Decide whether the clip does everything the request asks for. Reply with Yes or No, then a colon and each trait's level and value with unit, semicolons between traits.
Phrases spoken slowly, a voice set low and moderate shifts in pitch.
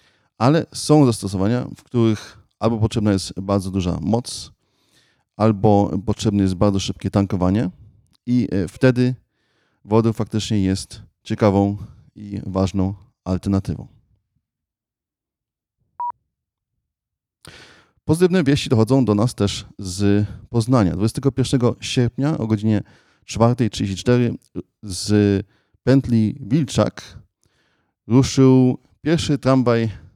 Yes: slow, 90 wpm; low, 110 Hz; average, 3.9 semitones